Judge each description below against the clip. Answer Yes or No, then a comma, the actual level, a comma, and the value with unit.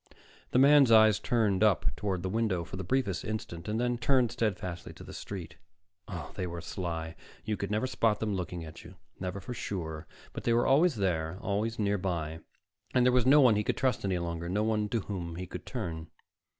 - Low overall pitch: Yes, low, 100 Hz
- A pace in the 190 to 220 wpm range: Yes, fast, 205 wpm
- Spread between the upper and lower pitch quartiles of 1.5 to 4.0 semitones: No, average, 4.6 semitones